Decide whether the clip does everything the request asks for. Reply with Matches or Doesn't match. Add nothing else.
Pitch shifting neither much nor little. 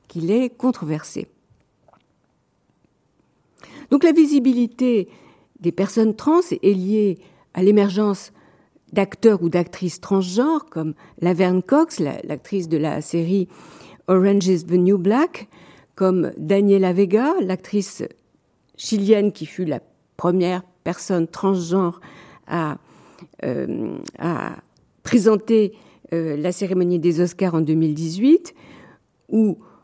Matches